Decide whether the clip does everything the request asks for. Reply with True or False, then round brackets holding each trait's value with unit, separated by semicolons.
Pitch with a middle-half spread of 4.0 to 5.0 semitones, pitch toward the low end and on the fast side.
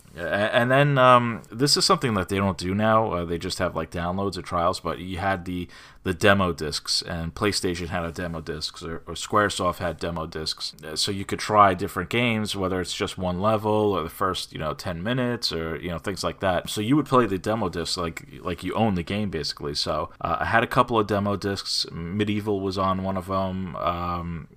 False (3.3 semitones; 95 Hz; 225 wpm)